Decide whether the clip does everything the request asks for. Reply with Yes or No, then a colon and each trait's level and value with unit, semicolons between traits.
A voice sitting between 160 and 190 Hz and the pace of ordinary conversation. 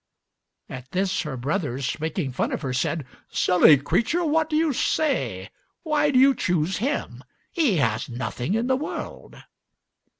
Yes: medium, 185 Hz; average, 155 wpm